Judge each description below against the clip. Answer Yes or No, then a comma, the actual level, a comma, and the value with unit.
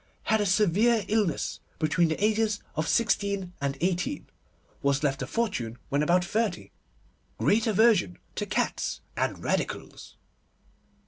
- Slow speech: Yes, slow, 125 wpm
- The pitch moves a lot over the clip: Yes, wide, 6.0 semitones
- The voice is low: No, high, 190 Hz